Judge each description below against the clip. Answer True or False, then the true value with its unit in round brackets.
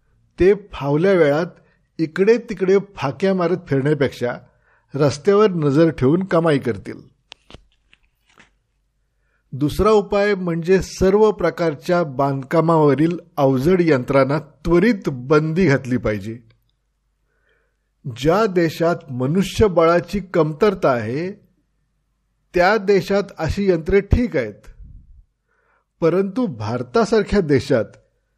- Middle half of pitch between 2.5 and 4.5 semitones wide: False (5.5 semitones)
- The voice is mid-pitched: True (165 Hz)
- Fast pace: False (80 wpm)